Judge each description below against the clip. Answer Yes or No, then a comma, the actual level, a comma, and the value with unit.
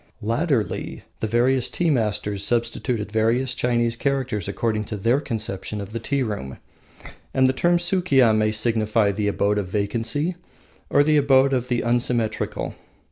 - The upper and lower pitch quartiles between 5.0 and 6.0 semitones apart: No, average, 3.7 semitones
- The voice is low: Yes, low, 115 Hz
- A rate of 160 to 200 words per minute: No, average, 150 wpm